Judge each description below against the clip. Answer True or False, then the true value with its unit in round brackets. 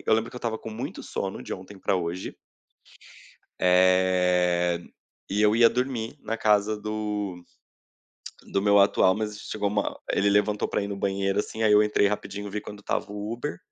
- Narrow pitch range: True (1.9 semitones)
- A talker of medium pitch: False (105 Hz)